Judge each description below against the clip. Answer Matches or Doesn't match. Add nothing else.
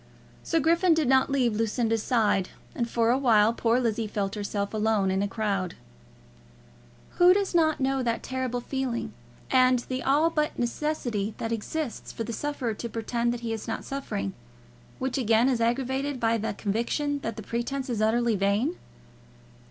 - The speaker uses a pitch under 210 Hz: Doesn't match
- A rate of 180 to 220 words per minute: Doesn't match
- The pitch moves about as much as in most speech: Matches